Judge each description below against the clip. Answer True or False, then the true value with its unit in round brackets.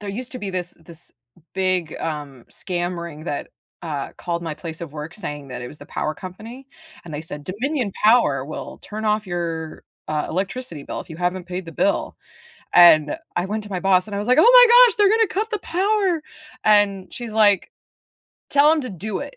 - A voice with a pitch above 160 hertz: True (190 Hz)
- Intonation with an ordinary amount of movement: False (7.0 semitones)